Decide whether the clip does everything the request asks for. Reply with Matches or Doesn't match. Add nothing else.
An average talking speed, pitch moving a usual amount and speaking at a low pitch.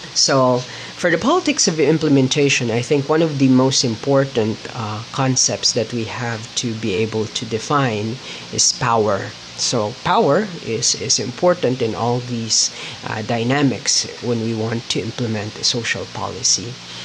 Matches